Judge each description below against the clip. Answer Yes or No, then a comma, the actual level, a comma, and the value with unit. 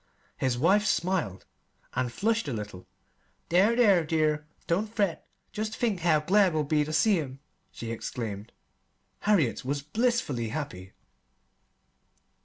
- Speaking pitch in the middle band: Yes, medium, 155 Hz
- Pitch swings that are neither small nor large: No, wide, 8.0 semitones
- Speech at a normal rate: No, slow, 130 wpm